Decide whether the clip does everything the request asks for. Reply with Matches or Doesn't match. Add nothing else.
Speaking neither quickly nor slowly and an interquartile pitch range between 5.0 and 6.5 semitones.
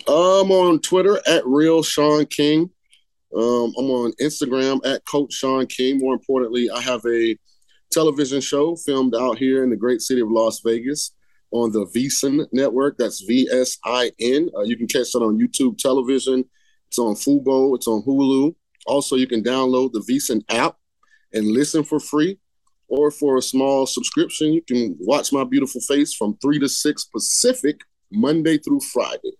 Doesn't match